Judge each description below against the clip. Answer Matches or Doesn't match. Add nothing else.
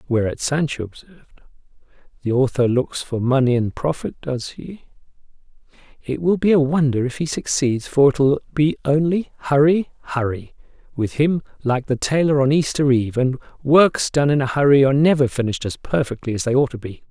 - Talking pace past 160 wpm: Matches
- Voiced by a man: Matches